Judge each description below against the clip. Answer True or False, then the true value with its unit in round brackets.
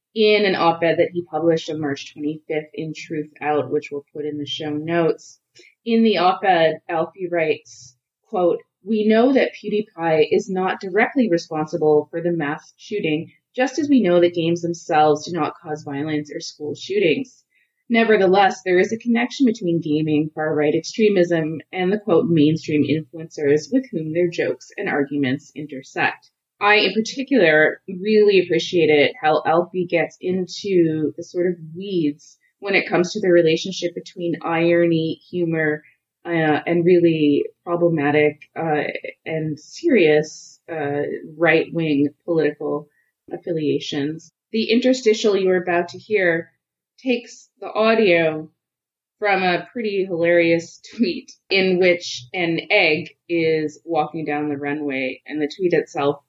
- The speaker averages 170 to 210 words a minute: False (140 wpm)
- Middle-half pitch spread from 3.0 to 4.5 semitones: True (3.8 semitones)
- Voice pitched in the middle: True (165 Hz)